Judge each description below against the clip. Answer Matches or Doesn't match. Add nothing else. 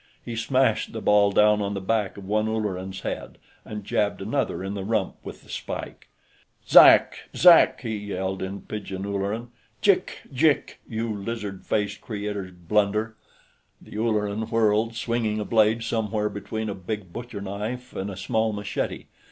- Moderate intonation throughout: Doesn't match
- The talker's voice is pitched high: Doesn't match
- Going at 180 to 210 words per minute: Doesn't match